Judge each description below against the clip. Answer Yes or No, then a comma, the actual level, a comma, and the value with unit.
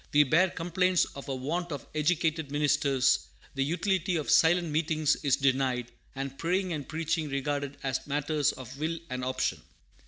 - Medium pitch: Yes, medium, 150 Hz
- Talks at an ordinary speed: Yes, average, 160 wpm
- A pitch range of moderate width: Yes, average, 3.3 semitones